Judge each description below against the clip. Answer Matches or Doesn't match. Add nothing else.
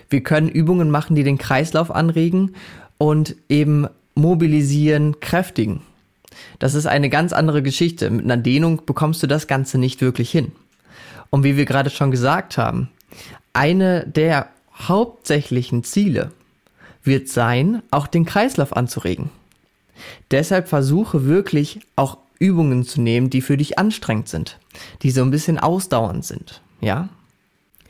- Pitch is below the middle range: Doesn't match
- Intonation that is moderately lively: Matches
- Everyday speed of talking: Matches